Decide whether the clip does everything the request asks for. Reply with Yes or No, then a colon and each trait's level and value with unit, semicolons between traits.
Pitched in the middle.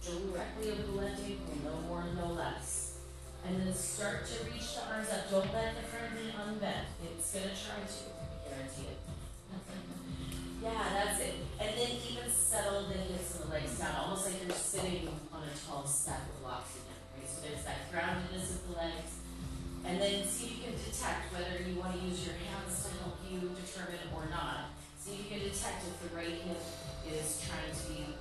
Yes: medium, 170 Hz